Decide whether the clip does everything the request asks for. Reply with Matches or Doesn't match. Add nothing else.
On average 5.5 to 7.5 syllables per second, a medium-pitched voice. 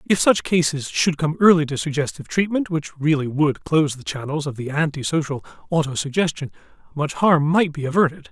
Matches